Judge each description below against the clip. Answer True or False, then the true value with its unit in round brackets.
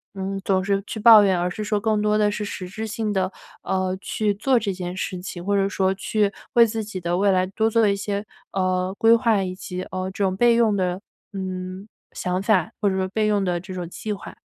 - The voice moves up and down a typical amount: False (2.3 semitones)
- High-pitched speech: True (195 Hz)